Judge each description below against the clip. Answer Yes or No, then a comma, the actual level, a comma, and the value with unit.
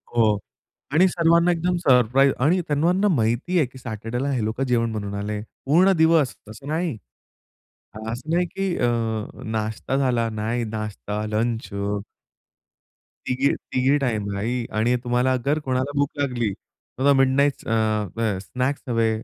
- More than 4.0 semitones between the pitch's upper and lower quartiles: Yes, average, 4.4 semitones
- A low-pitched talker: Yes, low, 125 Hz